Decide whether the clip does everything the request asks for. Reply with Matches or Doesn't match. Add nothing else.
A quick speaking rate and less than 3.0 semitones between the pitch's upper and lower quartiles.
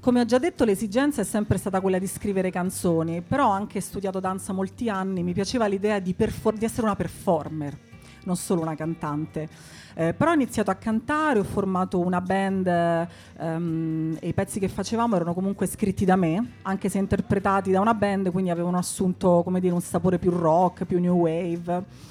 Doesn't match